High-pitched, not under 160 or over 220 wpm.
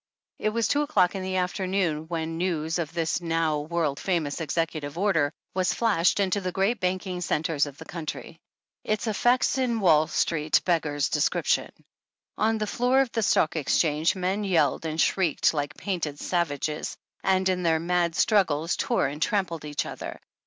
No: medium, 170 Hz; average, 165 wpm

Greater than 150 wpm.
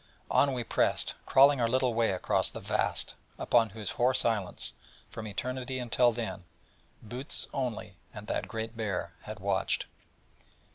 No: average, 145 wpm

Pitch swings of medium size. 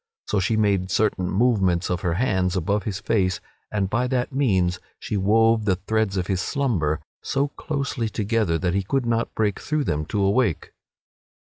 Yes: average, 3.8 semitones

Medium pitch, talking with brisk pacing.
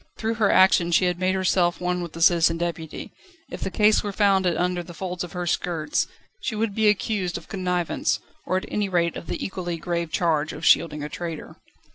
Yes: medium, 180 Hz; fast, 210 wpm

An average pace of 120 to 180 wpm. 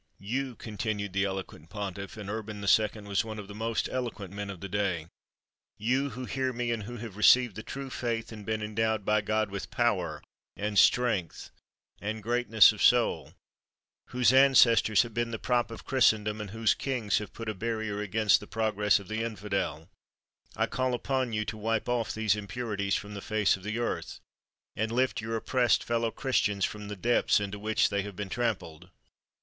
No: average, 190 wpm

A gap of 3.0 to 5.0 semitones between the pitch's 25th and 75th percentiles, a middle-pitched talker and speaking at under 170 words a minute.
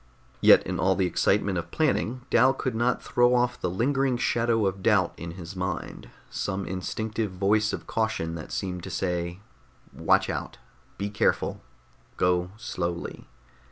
No: average, 4.3 semitones; low, 100 Hz; average, 155 wpm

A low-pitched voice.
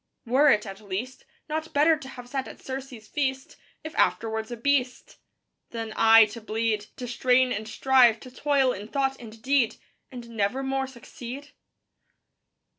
No: very high, 250 Hz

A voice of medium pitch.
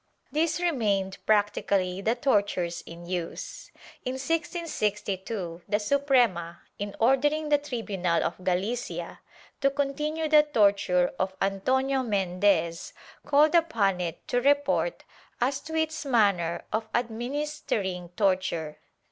No: high, 220 Hz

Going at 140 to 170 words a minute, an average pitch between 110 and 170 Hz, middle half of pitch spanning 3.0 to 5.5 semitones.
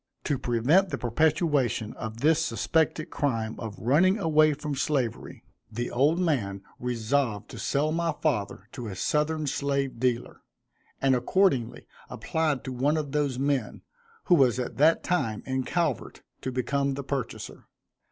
Yes: average, 150 wpm; medium, 140 Hz; average, 4.2 semitones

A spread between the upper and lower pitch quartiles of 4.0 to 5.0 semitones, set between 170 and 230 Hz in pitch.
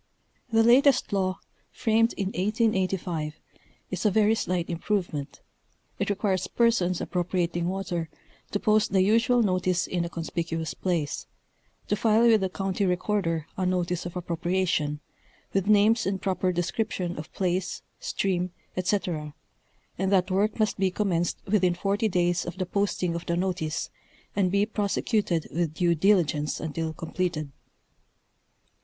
No: average, 2.8 semitones; medium, 185 Hz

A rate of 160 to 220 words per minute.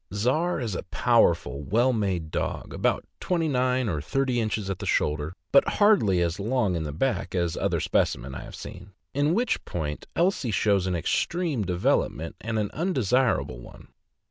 Yes: average, 170 wpm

